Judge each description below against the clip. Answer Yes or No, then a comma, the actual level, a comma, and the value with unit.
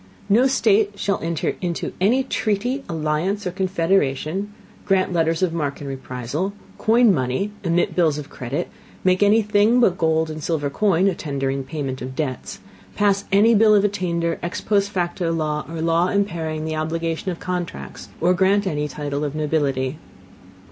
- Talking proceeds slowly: No, average, 170 wpm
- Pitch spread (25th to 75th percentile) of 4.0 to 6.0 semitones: Yes, average, 4.6 semitones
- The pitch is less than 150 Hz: No, medium, 170 Hz